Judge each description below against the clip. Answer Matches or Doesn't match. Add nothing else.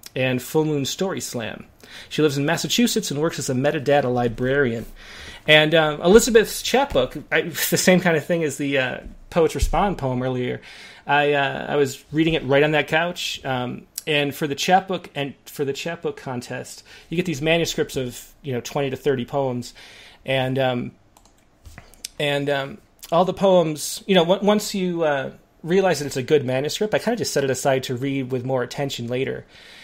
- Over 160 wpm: Matches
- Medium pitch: Matches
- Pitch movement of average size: Matches